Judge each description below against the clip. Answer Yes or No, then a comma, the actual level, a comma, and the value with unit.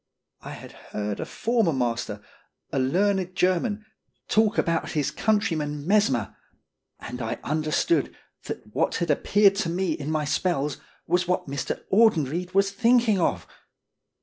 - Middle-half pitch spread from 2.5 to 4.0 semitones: No, wide, 5.5 semitones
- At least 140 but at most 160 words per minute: Yes, average, 145 wpm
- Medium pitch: Yes, medium, 170 Hz